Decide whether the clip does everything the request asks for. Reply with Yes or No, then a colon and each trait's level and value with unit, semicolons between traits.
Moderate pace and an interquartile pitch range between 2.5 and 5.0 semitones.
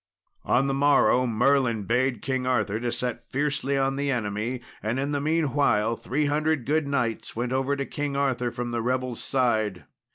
Yes: average, 175 wpm; average, 2.9 semitones